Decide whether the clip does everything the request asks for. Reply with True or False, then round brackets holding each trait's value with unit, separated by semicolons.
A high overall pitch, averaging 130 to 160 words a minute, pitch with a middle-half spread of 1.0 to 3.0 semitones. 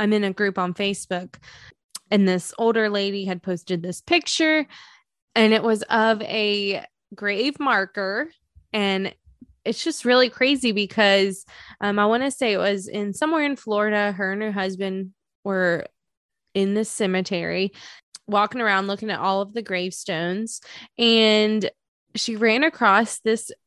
True (205 Hz; 150 wpm; 2.7 semitones)